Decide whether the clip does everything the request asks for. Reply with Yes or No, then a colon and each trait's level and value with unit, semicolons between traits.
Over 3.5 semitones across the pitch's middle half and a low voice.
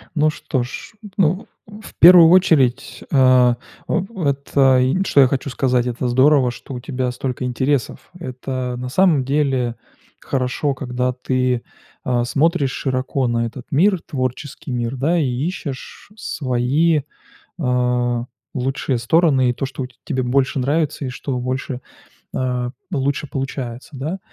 No: average, 2.7 semitones; low, 130 Hz